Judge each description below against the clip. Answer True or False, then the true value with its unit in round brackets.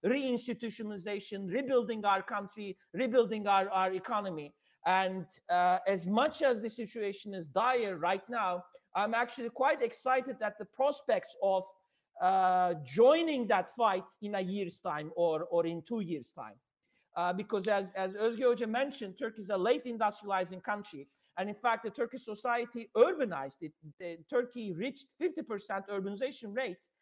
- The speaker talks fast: True (150 wpm)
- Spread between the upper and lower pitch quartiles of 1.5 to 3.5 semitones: False (4.3 semitones)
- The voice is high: True (210 Hz)